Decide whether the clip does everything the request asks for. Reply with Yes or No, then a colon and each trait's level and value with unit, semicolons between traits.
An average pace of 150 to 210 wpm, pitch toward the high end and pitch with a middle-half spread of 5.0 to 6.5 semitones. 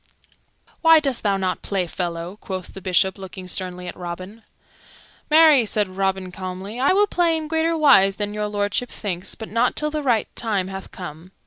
Yes: average, 185 wpm; high, 200 Hz; wide, 5.4 semitones